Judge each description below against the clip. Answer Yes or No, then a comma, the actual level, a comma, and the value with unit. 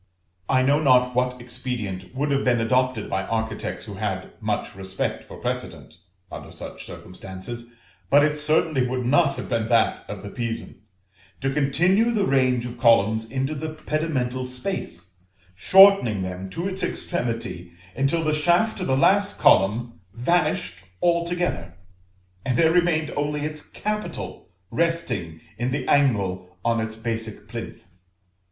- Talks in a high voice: No, low, 130 Hz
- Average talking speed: Yes, average, 145 wpm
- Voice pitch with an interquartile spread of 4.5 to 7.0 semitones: Yes, wide, 5.5 semitones